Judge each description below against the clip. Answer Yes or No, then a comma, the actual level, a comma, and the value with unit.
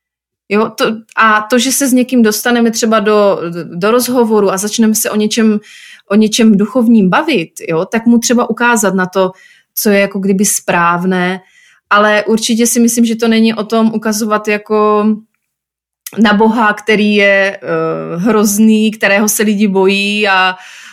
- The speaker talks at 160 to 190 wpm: Yes, fast, 165 wpm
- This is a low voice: No, high, 215 Hz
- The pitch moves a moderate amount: No, narrow, 2.3 semitones